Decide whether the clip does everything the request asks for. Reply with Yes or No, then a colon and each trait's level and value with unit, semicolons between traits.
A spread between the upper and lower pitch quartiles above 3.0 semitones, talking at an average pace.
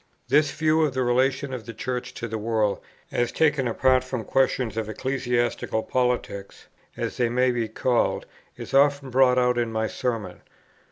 No: narrow, 2.4 semitones; average, 170 wpm